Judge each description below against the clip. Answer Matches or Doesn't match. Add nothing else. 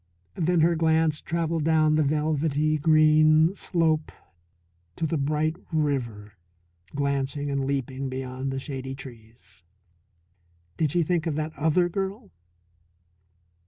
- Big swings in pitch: Doesn't match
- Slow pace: Matches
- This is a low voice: Doesn't match